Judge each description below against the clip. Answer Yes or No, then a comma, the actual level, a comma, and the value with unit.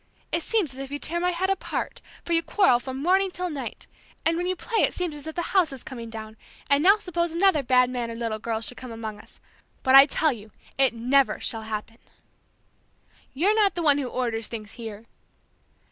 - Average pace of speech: No, fast, 215 wpm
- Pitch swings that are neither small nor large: No, wide, 6.9 semitones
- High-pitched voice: Yes, very high, 275 Hz